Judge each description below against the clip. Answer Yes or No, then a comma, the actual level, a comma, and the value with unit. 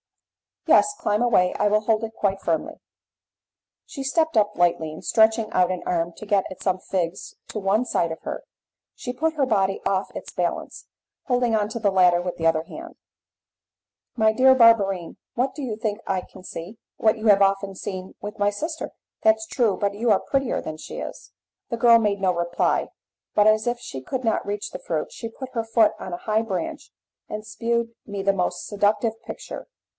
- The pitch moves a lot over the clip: No, average, 3.4 semitones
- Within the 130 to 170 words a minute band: No, average, 200 wpm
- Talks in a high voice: Yes, high, 210 Hz